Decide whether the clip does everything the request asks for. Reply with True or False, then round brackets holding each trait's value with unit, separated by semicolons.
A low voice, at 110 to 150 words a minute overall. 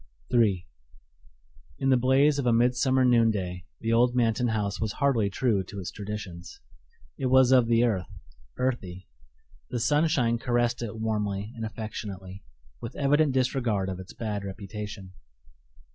True (115 Hz; 145 wpm)